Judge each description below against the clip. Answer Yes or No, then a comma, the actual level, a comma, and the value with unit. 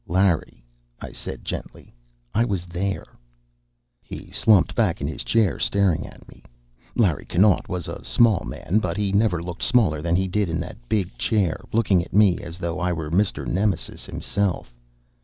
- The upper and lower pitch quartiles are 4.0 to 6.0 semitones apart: No, average, 3.5 semitones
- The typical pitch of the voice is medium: No, very low, 95 Hz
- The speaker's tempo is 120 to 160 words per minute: No, average, 175 wpm